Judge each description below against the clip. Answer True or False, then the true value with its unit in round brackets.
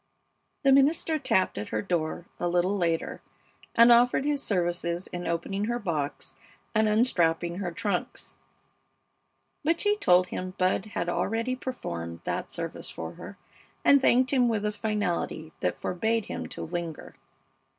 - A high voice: True (195 Hz)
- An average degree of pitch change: False (5.7 semitones)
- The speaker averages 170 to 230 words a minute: False (150 wpm)